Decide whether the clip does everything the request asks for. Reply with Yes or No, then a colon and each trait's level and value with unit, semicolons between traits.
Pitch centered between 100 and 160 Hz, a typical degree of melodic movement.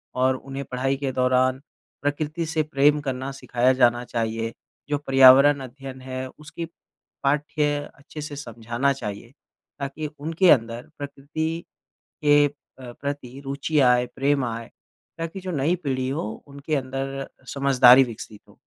No: low, 135 Hz; narrow, 2.3 semitones